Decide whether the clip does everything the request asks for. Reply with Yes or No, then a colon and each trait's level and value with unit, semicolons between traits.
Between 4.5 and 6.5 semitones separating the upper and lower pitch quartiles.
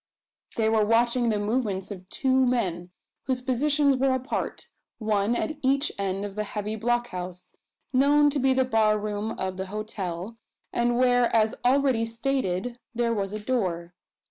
No: average, 3.9 semitones